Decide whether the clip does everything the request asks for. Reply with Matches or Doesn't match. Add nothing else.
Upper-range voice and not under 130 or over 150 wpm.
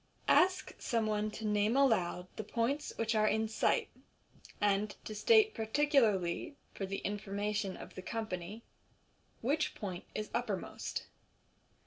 Matches